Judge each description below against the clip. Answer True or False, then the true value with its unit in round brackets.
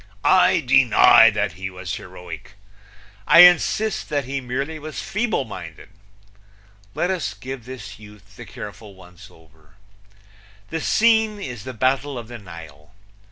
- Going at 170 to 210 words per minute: False (140 wpm)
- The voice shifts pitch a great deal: True (8.1 semitones)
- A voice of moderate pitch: False (120 Hz)